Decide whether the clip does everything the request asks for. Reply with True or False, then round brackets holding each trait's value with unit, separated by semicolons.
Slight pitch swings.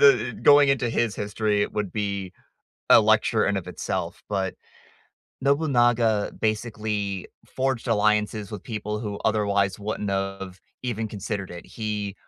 True (2.2 semitones)